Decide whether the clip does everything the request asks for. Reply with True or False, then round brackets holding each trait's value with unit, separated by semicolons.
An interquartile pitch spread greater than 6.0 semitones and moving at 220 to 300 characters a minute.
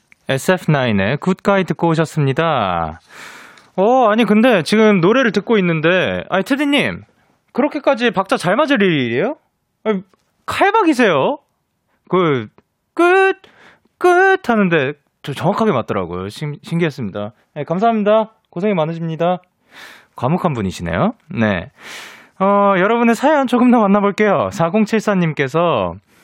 True (6.6 semitones; 265 characters per minute)